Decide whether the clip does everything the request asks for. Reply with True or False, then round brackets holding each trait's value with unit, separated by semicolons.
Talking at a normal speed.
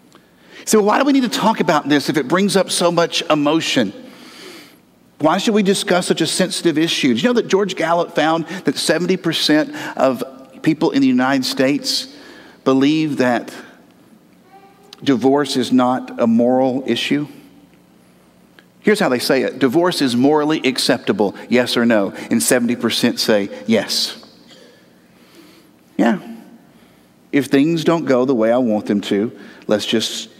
True (150 wpm)